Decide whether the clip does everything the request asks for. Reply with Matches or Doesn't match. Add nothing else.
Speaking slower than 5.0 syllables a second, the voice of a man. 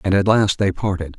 Doesn't match